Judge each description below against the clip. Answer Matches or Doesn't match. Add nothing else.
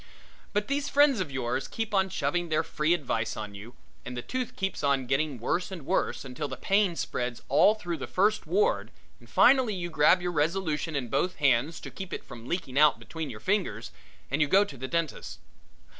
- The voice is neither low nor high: Matches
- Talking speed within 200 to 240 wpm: Matches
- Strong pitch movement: Matches